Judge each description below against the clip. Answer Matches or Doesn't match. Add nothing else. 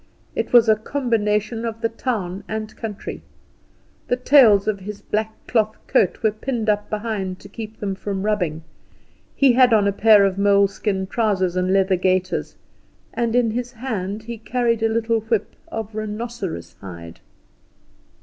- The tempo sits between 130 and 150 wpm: Doesn't match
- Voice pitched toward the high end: Matches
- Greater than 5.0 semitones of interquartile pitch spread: Doesn't match